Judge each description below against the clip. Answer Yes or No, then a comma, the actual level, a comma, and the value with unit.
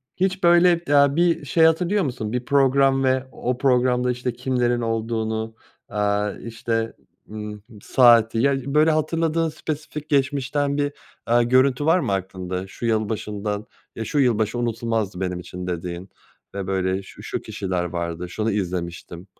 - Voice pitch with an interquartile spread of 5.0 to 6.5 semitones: Yes, wide, 5.4 semitones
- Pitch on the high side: No, low, 120 Hz